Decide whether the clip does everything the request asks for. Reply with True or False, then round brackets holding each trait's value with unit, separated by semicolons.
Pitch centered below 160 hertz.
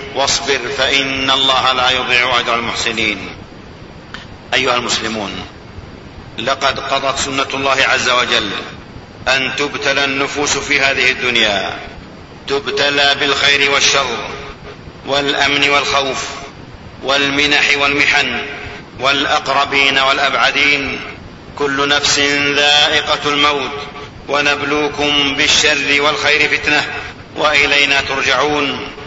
True (140 Hz)